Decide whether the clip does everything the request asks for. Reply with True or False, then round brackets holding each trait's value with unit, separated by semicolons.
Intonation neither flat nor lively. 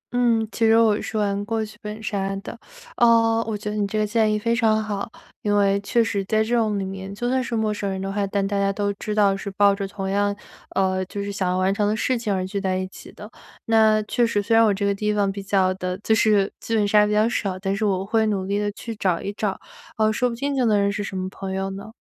False (1.9 semitones)